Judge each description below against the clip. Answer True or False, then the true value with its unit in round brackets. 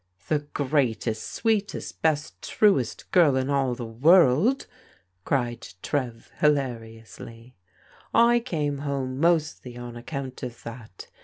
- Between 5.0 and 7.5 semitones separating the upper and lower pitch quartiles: False (4.4 semitones)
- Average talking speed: False (125 wpm)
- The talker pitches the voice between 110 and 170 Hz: True (135 Hz)